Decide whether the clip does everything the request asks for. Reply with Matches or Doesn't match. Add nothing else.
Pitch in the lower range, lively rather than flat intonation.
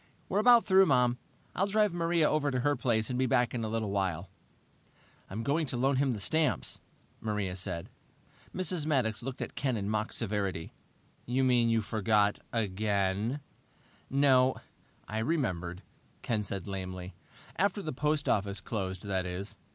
Matches